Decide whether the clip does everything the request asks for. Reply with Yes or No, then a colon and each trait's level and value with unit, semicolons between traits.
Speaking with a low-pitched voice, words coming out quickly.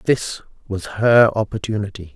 No: low, 105 Hz; slow, 110 wpm